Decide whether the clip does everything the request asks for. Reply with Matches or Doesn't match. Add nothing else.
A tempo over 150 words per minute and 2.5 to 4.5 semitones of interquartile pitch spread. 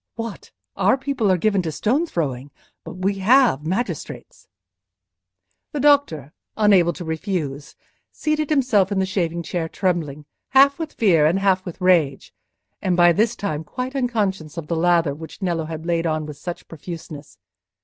Doesn't match